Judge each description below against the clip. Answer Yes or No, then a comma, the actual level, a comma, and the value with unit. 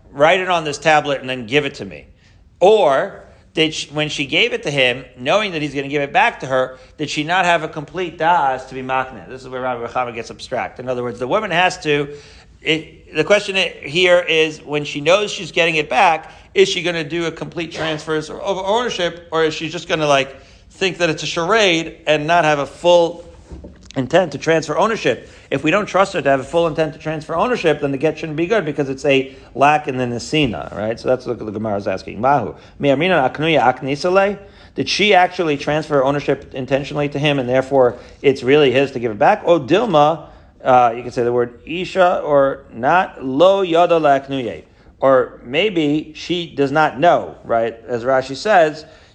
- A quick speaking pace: Yes, fast, 210 wpm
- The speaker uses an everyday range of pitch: Yes, average, 4.2 semitones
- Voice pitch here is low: No, medium, 150 Hz